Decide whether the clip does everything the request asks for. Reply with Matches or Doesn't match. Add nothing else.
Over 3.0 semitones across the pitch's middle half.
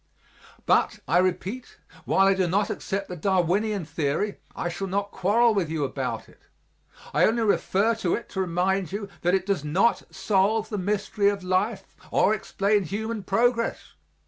Doesn't match